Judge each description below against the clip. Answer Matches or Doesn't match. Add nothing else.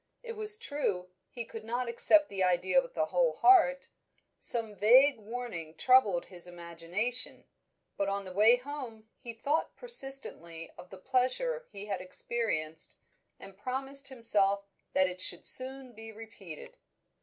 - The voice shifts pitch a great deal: Matches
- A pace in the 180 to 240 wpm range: Doesn't match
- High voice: Matches